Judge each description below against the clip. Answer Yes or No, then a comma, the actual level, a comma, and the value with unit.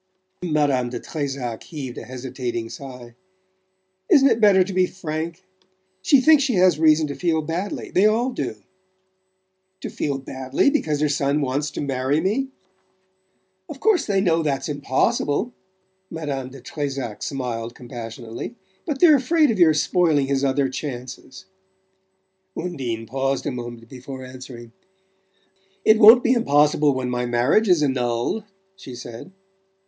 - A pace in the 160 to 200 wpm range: No, average, 145 wpm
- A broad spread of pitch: Yes, wide, 6.3 semitones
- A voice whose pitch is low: No, medium, 145 Hz